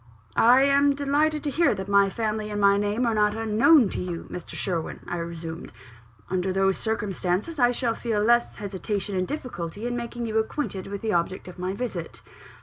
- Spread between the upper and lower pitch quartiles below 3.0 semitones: No, average, 4.3 semitones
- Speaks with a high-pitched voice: Yes, high, 210 Hz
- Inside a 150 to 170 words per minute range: No, average, 190 wpm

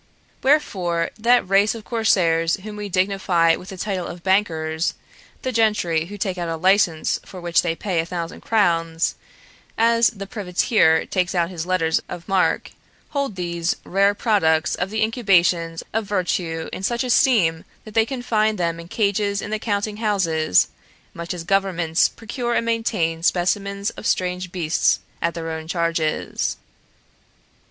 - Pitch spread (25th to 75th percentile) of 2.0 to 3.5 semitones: No, average, 4.0 semitones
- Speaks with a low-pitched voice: No, medium, 185 Hz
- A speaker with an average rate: Yes, average, 155 wpm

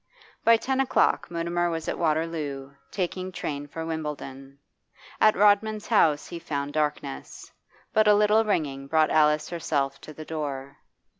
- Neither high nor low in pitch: Yes, medium, 160 Hz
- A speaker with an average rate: Yes, average, 145 wpm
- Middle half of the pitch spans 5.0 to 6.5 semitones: No, average, 4.4 semitones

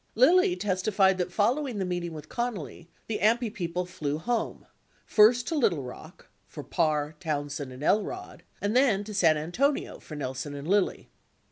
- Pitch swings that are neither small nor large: No, wide, 7.0 semitones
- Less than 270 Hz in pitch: Yes, high, 190 Hz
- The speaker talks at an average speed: Yes, average, 165 wpm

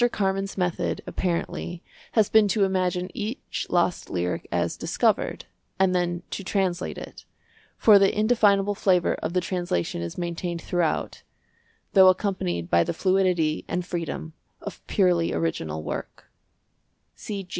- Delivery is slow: Yes, slow, 130 wpm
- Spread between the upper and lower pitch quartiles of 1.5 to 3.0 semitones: Yes, narrow, 2.5 semitones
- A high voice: No, medium, 180 Hz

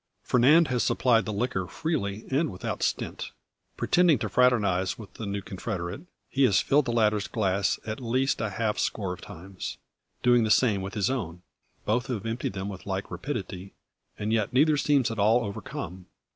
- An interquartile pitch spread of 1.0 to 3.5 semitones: No, average, 4.3 semitones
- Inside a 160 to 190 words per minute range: Yes, average, 180 wpm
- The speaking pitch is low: Yes, low, 110 Hz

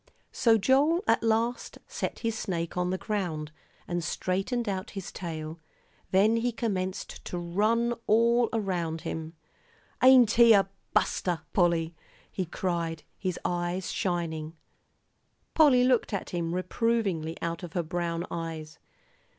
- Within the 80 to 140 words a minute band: Yes, slow, 135 wpm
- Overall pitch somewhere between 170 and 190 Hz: Yes, medium, 185 Hz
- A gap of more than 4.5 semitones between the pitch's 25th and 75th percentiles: Yes, average, 5.1 semitones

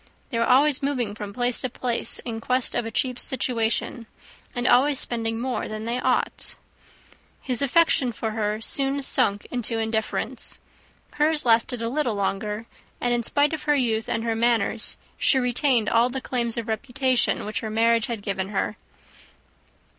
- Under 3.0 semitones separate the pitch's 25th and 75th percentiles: Yes, narrow, 2.5 semitones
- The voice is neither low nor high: No, high, 235 Hz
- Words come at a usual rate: Yes, average, 170 wpm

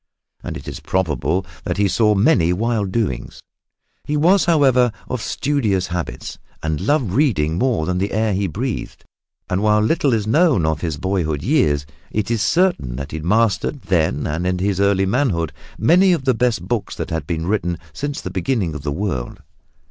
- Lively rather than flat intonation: Yes, wide, 7.0 semitones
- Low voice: Yes, low, 100 Hz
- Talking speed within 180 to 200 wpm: Yes, average, 185 wpm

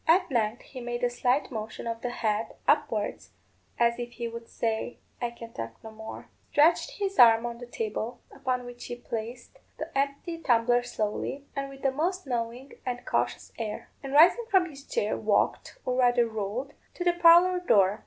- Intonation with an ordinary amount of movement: Yes, average, 3.5 semitones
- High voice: Yes, high, 245 Hz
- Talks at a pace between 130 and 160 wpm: No, average, 185 wpm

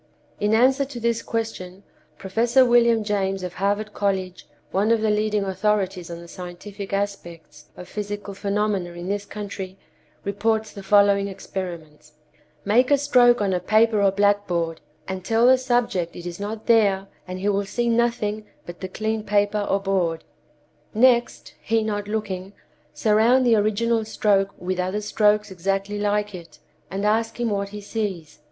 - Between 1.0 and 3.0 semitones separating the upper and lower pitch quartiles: Yes, narrow, 2.5 semitones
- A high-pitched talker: Yes, high, 205 Hz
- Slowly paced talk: No, average, 160 wpm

